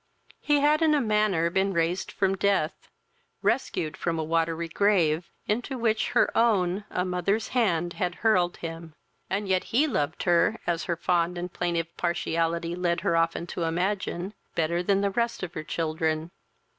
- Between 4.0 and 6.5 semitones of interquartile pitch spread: No, average, 3.3 semitones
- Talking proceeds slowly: No, average, 170 wpm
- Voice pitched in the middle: Yes, medium, 175 Hz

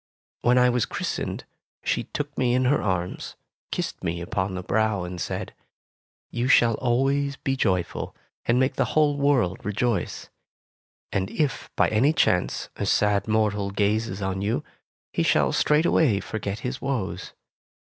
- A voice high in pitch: No, low, 110 Hz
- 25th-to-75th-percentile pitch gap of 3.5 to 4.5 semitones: No, average, 5.1 semitones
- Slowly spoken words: No, average, 150 wpm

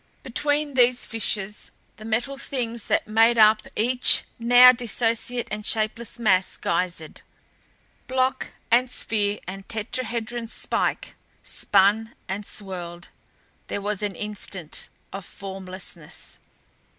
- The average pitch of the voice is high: Yes, high, 220 Hz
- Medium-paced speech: No, slow, 110 wpm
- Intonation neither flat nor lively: Yes, average, 3.5 semitones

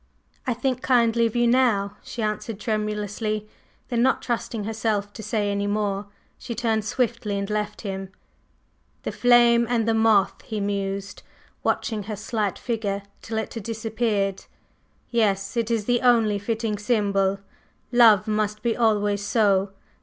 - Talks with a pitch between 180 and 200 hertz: No, high, 215 Hz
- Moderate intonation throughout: No, narrow, 2.3 semitones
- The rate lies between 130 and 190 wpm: Yes, average, 150 wpm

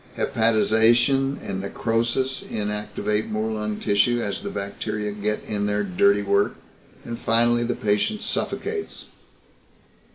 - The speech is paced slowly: Yes, slow, 120 wpm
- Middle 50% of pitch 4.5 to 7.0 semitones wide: No, narrow, 2.5 semitones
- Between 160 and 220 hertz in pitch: No, low, 110 Hz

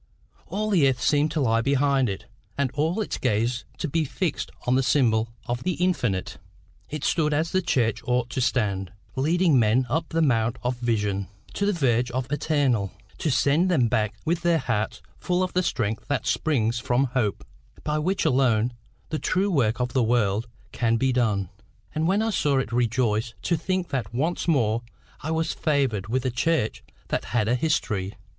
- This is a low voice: Yes, low, 130 Hz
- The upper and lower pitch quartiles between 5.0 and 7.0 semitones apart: Yes, wide, 5.5 semitones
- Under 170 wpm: No, average, 190 wpm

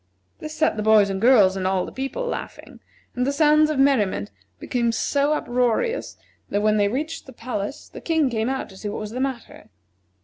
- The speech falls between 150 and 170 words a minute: No, fast, 205 wpm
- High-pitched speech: Yes, high, 245 Hz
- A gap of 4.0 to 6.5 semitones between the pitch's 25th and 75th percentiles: Yes, average, 5.2 semitones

